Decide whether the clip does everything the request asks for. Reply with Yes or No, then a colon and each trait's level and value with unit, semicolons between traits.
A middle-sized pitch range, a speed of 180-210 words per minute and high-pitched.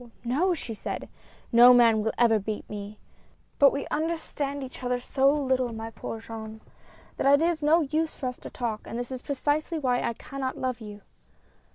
Yes: average, 3.9 semitones; average, 190 wpm; very high, 255 Hz